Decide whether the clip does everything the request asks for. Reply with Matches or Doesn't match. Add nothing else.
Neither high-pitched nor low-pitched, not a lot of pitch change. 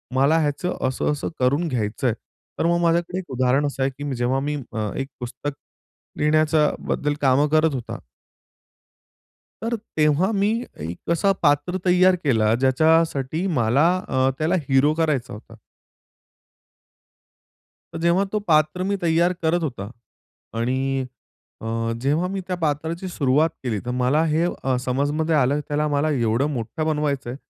Doesn't match